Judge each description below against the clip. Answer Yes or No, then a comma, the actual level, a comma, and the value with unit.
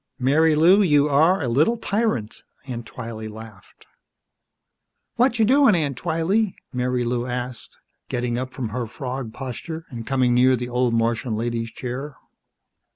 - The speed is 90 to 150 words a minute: Yes, slow, 135 wpm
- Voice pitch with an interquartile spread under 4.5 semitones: No, average, 5.1 semitones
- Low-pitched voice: Yes, low, 125 Hz